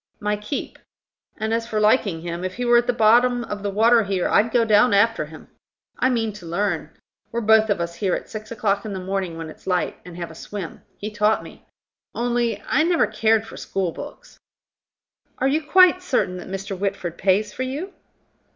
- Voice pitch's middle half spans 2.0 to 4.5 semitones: Yes, average, 3.9 semitones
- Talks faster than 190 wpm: Yes, fast, 205 wpm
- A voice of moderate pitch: No, high, 210 Hz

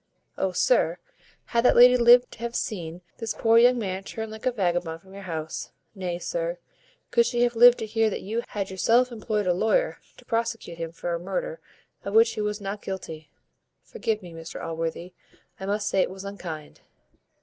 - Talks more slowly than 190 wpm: No, average, 195 wpm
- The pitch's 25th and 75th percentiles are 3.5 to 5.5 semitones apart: Yes, average, 4.7 semitones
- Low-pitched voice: No, high, 205 Hz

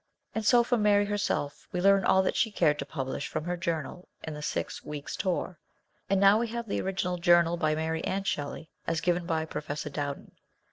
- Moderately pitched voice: Yes, medium, 175 Hz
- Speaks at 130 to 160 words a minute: No, fast, 205 wpm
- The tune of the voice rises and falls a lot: No, average, 4.2 semitones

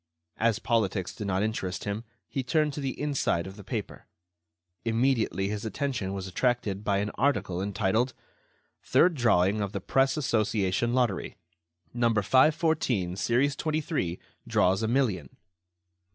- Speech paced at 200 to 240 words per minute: No, average, 140 wpm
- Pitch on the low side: Yes, low, 110 Hz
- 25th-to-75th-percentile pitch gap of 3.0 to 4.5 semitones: No, average, 5.3 semitones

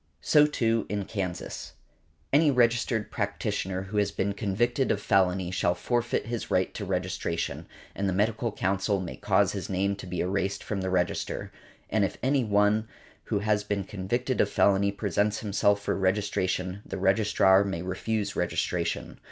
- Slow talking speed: No, average, 160 wpm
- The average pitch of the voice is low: Yes, low, 100 Hz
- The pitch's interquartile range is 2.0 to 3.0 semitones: Yes, narrow, 2.5 semitones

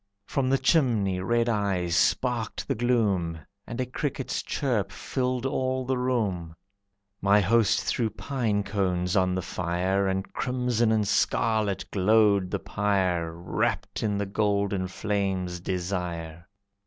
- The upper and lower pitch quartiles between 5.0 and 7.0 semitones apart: No, average, 4.2 semitones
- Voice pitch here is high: No, low, 100 Hz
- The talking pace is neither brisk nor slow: No, slow, 130 wpm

